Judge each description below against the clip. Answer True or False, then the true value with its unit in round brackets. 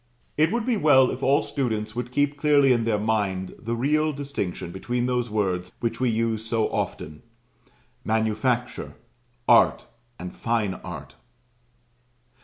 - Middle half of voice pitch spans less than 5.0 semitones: True (4.0 semitones)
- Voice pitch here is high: False (115 Hz)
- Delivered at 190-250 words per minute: False (140 wpm)